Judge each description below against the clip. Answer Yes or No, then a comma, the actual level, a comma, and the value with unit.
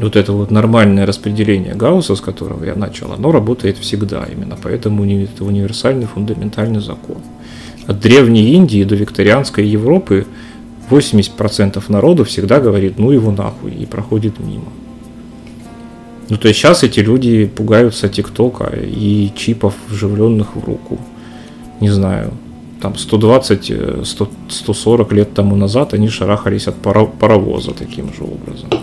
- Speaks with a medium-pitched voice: No, low, 105 Hz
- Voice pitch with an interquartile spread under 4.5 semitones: Yes, narrow, 2.4 semitones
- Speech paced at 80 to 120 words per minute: No, average, 135 wpm